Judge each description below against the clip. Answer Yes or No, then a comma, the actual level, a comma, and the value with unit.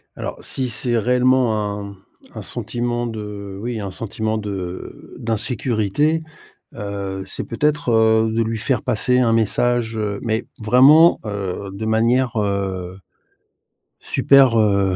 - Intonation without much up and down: No, average, 3.2 semitones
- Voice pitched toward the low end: Yes, low, 110 Hz